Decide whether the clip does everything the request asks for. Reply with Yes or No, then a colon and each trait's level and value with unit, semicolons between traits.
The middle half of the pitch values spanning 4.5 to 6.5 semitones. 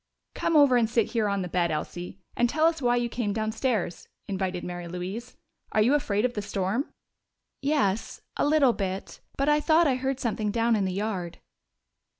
Yes: average, 5.3 semitones